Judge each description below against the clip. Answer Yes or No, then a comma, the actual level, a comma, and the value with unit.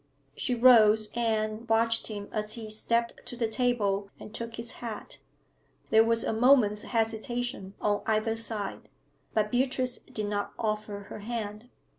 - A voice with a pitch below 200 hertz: No, high, 225 Hz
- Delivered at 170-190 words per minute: No, average, 150 wpm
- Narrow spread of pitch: Yes, narrow, 1.8 semitones